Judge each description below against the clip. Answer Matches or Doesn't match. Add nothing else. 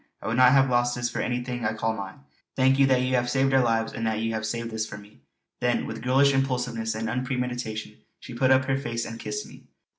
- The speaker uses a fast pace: Matches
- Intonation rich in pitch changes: Doesn't match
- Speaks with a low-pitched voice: Matches